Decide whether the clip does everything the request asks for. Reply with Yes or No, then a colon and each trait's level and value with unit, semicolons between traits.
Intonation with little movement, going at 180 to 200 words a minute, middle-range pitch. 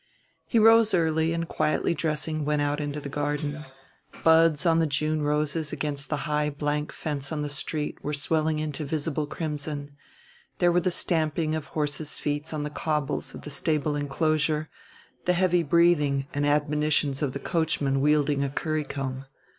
No: narrow, 1.6 semitones; average, 165 wpm; medium, 150 Hz